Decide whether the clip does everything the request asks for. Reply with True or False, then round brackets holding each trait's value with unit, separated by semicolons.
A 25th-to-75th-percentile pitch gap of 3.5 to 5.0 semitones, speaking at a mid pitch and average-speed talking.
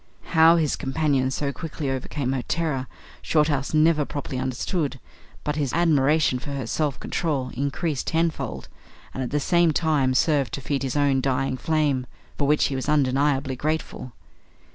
False (2.8 semitones; 145 Hz; 160 wpm)